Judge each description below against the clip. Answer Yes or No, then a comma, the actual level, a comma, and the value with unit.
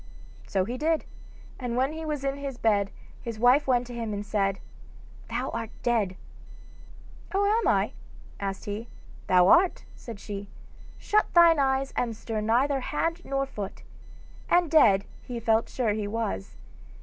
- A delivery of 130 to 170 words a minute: Yes, average, 160 wpm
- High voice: Yes, high, 235 Hz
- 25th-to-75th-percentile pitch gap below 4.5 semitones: No, average, 4.8 semitones